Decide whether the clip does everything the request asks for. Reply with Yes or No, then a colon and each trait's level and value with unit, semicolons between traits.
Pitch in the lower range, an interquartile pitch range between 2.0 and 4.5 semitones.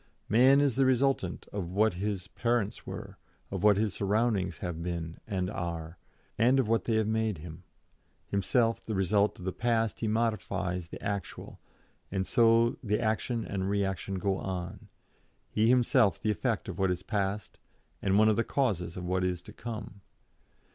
Yes: low, 100 Hz; average, 3.5 semitones